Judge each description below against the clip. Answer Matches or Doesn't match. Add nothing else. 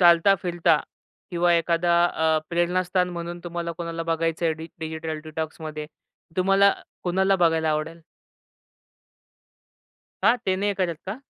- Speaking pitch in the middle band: Matches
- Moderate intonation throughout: Doesn't match